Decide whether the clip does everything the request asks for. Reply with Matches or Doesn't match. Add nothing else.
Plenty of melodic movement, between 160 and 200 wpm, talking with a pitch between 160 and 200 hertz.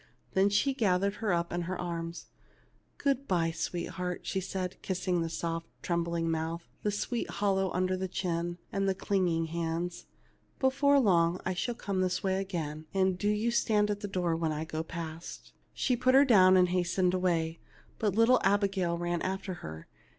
Doesn't match